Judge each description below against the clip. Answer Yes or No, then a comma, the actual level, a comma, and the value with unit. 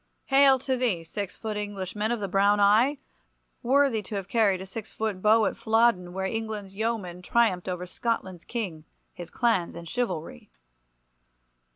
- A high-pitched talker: Yes, high, 210 Hz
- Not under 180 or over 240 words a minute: No, average, 160 wpm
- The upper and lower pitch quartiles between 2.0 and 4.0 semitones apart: Yes, average, 3.7 semitones